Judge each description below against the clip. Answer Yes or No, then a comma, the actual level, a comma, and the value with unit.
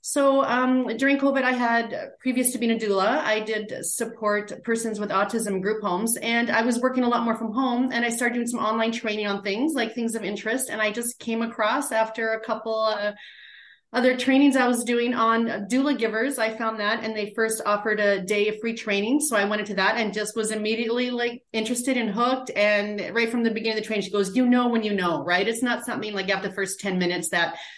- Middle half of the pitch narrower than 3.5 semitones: Yes, narrow, 2.4 semitones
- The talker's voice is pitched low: No, high, 225 Hz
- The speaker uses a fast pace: Yes, fast, 235 wpm